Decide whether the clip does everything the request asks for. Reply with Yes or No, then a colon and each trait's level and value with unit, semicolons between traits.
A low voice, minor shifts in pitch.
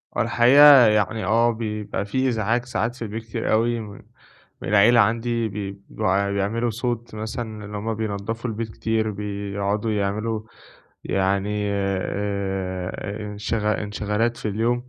Yes: low, 105 Hz; narrow, 2.2 semitones